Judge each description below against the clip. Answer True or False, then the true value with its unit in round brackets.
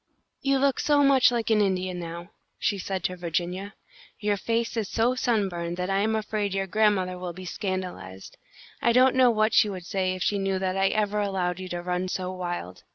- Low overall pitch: False (195 Hz)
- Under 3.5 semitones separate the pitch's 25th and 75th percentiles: True (3.0 semitones)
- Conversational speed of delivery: False (210 wpm)